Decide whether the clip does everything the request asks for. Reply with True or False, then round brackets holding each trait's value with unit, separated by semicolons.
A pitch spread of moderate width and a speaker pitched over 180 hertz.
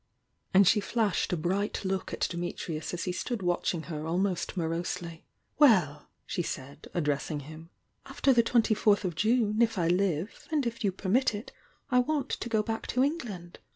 True (5.0 semitones; 190 Hz)